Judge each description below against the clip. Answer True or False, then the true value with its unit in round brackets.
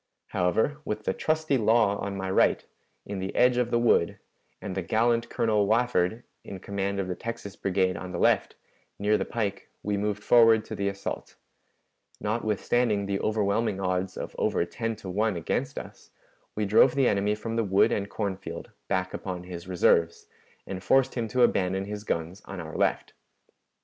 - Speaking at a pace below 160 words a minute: False (180 wpm)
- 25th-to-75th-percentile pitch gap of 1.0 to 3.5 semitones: True (3.1 semitones)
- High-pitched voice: False (100 Hz)